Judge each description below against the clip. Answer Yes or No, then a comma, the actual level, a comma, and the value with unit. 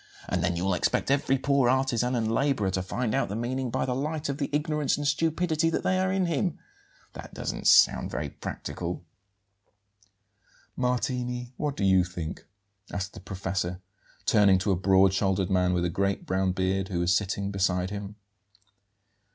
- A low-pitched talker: Yes, low, 105 Hz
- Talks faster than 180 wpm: No, average, 170 wpm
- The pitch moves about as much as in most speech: No, wide, 6.3 semitones